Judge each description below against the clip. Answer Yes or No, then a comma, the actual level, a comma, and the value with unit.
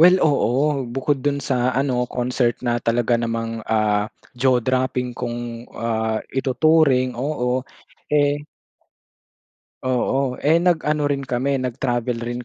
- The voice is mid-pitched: No, low, 125 Hz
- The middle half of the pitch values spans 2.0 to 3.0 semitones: Yes, average, 2.7 semitones